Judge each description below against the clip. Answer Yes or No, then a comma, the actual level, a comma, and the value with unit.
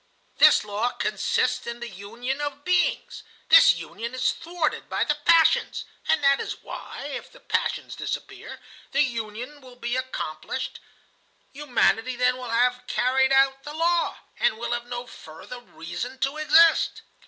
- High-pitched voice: Yes, very high, 250 Hz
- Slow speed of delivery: No, average, 155 wpm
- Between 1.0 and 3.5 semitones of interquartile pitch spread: Yes, average, 3.1 semitones